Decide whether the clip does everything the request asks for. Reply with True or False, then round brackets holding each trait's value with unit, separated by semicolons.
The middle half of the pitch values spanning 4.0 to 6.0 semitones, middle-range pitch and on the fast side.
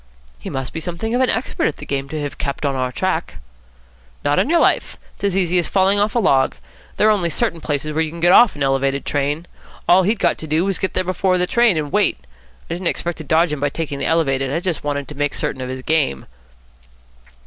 True (4.8 semitones; 160 Hz; 255 wpm)